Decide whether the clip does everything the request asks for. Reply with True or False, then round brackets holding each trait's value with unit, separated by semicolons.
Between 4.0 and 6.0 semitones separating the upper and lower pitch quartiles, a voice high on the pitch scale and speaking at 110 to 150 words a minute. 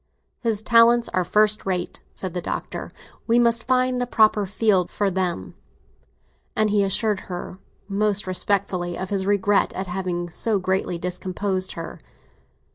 False (2.8 semitones; 195 Hz; 145 wpm)